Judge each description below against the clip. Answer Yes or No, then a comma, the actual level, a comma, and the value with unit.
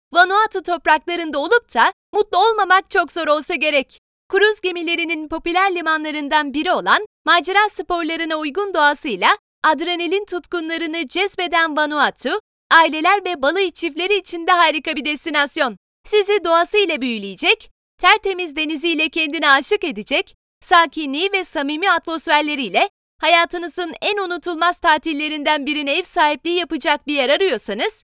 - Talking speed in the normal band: Yes, average, 120 wpm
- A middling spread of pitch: Yes, average, 3.3 semitones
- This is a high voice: Yes, very high, 335 Hz